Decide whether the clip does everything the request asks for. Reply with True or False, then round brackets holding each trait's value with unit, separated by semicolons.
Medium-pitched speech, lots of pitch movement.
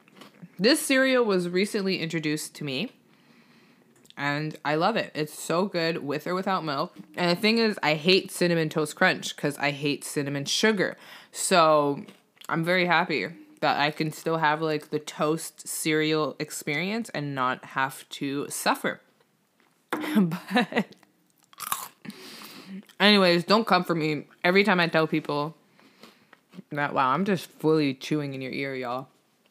False (165 Hz; 4.2 semitones)